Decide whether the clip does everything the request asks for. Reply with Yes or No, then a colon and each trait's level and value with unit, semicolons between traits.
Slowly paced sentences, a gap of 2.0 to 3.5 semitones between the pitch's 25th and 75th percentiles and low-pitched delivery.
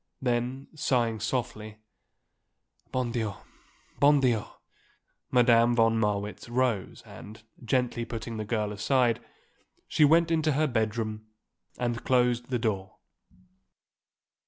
Yes: slow, 110 wpm; average, 2.7 semitones; low, 120 Hz